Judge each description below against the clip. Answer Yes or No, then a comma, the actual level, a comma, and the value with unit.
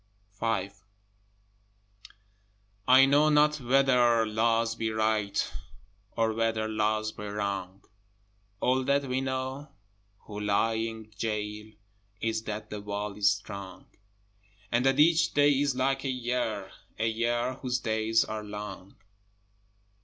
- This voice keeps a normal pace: No, slow, 125 wpm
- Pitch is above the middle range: No, low, 115 Hz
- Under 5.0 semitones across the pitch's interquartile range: Yes, average, 3.6 semitones